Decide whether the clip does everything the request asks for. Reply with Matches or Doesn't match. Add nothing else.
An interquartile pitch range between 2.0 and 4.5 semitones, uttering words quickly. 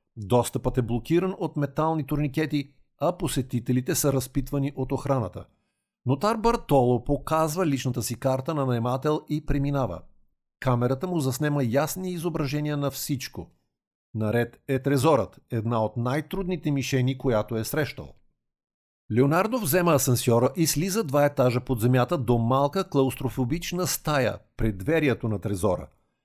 Doesn't match